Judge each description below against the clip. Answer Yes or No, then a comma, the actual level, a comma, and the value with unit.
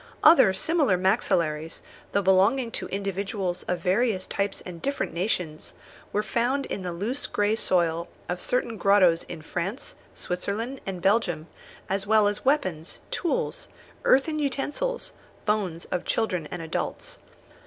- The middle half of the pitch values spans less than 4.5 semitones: No, average, 4.8 semitones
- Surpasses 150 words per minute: No, slow, 135 wpm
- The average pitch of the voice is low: No, high, 195 Hz